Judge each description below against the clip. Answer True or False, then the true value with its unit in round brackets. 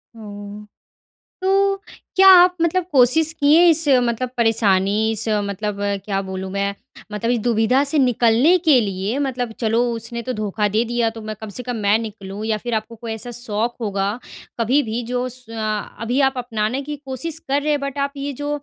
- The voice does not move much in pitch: False (4.1 semitones)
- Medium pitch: False (230 Hz)